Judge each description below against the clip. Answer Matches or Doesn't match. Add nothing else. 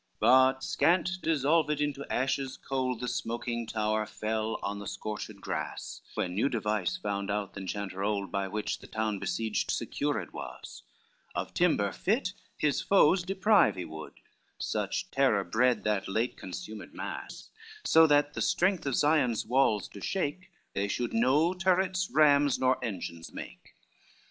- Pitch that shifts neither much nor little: Doesn't match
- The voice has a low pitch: Matches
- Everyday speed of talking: Matches